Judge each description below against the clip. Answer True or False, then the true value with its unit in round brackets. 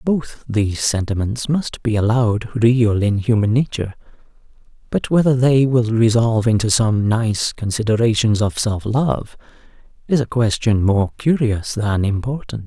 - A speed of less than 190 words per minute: True (135 wpm)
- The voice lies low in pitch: True (115 Hz)